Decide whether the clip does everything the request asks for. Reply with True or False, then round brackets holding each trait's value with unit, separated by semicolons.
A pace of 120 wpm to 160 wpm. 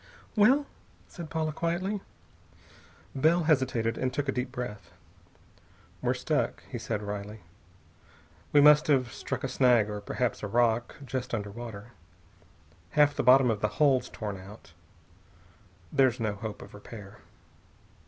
True (140 wpm)